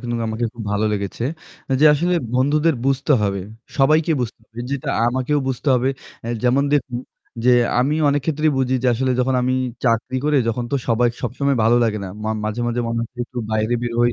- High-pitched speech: No, low, 125 Hz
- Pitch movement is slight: No, average, 3.3 semitones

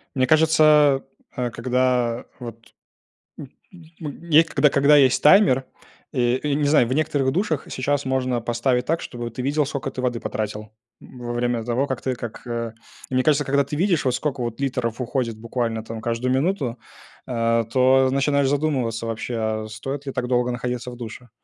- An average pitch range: Yes, average, 3.2 semitones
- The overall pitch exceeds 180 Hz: No, low, 130 Hz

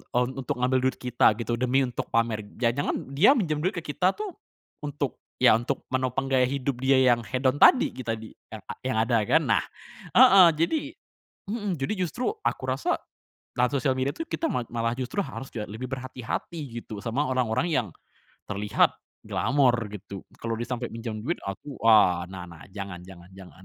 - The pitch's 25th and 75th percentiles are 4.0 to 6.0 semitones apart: No, average, 3.6 semitones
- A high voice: No, low, 125 Hz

